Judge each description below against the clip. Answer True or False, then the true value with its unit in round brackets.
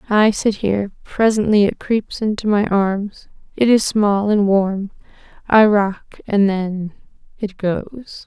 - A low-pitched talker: False (205 Hz)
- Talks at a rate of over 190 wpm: False (145 wpm)